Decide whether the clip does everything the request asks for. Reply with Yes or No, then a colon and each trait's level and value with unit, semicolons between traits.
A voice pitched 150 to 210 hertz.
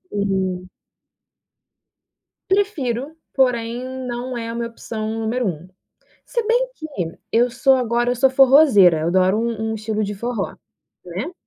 No: high, 235 Hz